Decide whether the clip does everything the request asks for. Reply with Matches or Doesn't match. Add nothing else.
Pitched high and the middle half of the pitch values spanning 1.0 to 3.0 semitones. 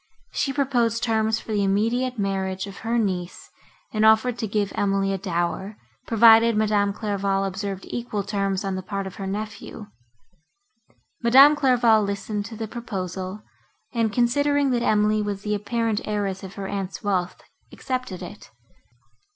Matches